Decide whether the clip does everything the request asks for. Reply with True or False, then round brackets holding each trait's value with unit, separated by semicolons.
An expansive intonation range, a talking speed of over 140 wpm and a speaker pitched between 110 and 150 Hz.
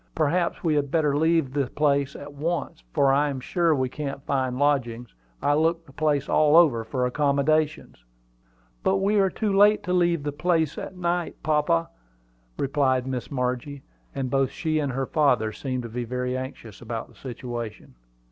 False (3.7 semitones; 175 wpm; 140 Hz)